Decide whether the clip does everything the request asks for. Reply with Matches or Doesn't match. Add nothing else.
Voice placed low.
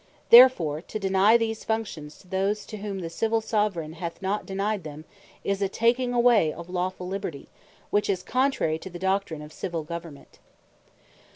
Doesn't match